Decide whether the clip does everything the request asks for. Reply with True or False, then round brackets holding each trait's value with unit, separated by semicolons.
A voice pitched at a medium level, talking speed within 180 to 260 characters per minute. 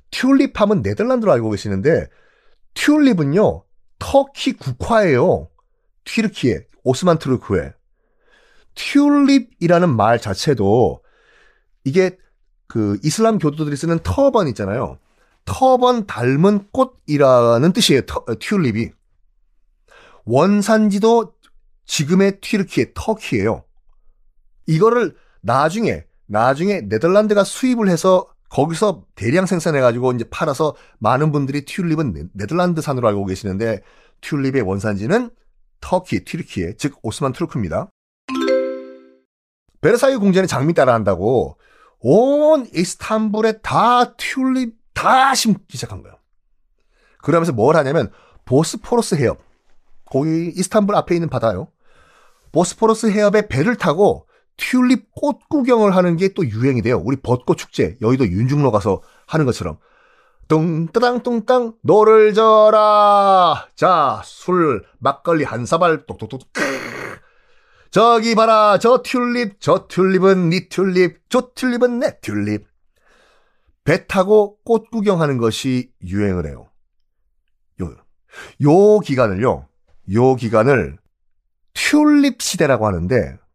True (175 Hz; 255 characters per minute)